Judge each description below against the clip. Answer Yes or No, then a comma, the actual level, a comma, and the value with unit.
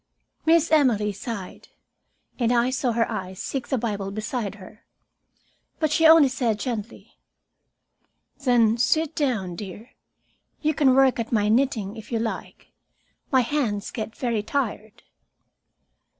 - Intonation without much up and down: No, average, 4.1 semitones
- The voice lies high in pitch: Yes, high, 235 Hz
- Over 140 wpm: No, slow, 135 wpm